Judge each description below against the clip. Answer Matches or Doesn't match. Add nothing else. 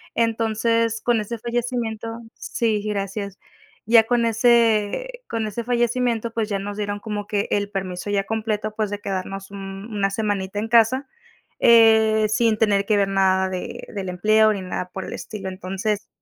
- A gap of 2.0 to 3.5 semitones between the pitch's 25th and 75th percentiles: Matches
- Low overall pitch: Doesn't match